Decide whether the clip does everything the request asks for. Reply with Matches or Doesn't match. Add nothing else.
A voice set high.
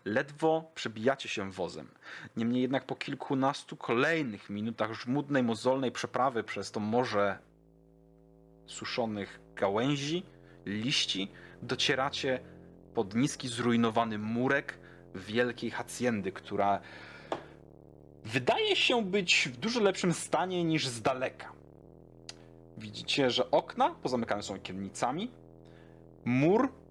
Doesn't match